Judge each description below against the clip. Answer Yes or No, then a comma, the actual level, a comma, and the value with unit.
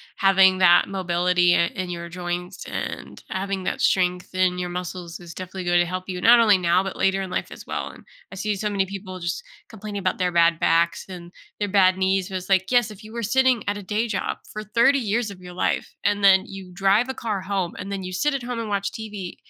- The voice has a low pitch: No, high, 190 Hz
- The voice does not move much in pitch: Yes, narrow, 2.3 semitones